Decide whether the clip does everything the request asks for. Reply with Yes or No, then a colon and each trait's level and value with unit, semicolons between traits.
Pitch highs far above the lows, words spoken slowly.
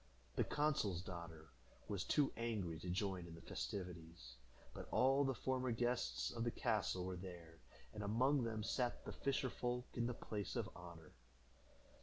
No: wide, 6.3 semitones; average, 165 wpm